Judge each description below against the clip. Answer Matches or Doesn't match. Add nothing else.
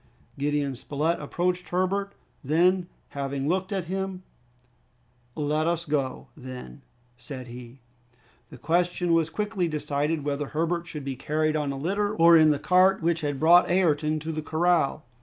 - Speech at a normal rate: Matches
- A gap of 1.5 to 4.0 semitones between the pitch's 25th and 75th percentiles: Matches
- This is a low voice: Doesn't match